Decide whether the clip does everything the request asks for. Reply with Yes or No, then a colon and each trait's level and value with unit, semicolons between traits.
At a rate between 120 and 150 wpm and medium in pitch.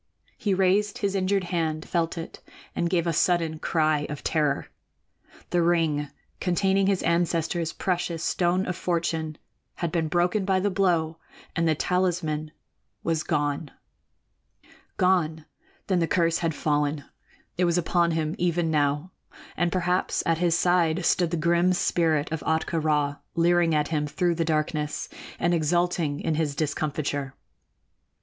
Yes: average, 145 wpm; medium, 165 Hz